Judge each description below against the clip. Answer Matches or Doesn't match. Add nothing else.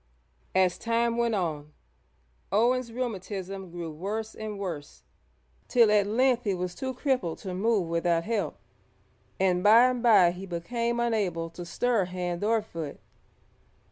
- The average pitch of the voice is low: Doesn't match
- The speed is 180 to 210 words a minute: Doesn't match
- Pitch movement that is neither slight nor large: Matches